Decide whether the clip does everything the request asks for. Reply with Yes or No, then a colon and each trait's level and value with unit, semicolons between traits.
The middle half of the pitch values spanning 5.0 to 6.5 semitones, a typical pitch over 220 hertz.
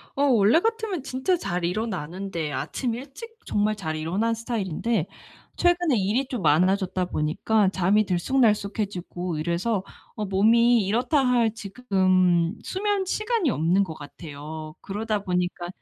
No: wide, 5.5 semitones; high, 205 Hz